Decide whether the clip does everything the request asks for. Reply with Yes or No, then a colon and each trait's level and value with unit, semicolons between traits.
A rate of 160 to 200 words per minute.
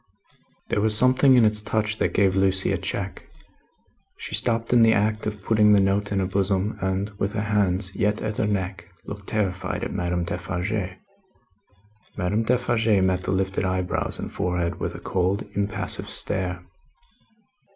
Yes: average, 165 wpm